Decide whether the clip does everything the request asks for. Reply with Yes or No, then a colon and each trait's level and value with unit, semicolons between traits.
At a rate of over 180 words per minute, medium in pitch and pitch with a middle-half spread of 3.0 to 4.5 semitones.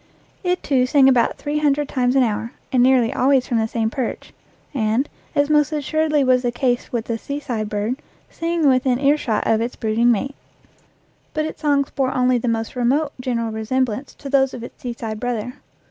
No: average, 190 wpm; very high, 255 Hz; average, 3.4 semitones